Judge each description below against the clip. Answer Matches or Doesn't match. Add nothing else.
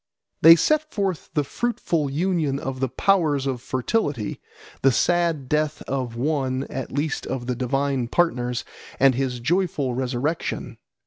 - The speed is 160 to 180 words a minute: Doesn't match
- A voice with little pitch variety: Doesn't match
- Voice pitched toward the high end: Doesn't match